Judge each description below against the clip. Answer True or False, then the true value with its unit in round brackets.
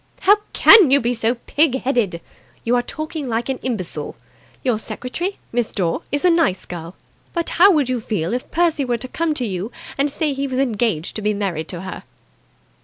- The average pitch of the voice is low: False (250 Hz)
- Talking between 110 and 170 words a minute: False (205 wpm)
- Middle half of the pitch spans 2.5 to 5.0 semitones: False (5.6 semitones)